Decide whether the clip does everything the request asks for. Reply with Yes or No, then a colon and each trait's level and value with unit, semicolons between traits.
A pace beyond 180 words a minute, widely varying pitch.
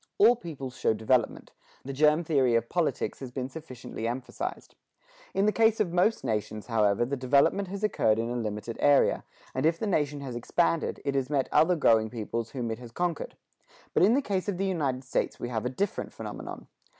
Yes: average, 200 wpm; wide, 6.7 semitones